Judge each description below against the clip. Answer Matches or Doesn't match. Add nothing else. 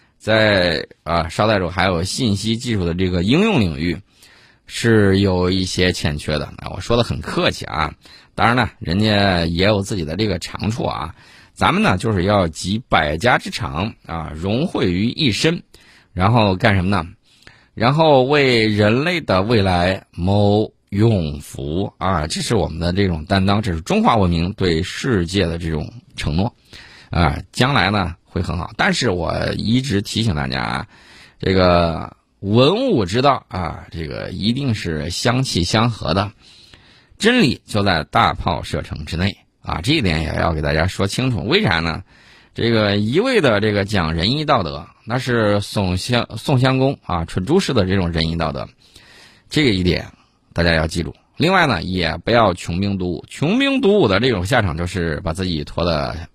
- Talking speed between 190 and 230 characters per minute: Doesn't match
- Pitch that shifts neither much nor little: Matches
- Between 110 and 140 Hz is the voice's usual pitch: Doesn't match